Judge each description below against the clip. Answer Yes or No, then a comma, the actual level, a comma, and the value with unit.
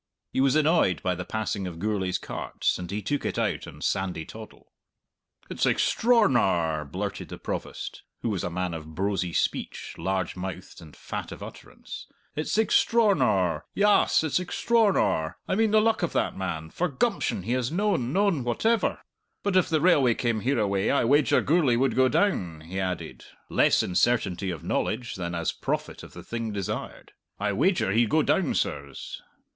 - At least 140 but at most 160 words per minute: No, average, 175 wpm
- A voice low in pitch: Yes, low, 115 Hz